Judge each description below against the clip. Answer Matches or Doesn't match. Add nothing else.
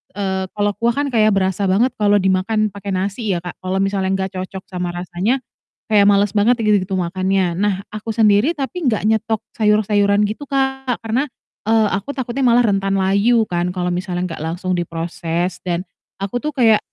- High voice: Matches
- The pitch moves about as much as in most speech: Matches